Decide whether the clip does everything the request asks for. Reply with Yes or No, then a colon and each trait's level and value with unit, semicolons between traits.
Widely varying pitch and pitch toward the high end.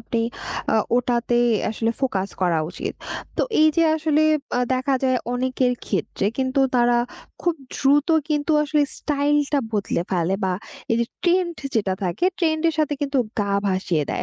Yes: wide, 6.0 semitones; very high, 260 Hz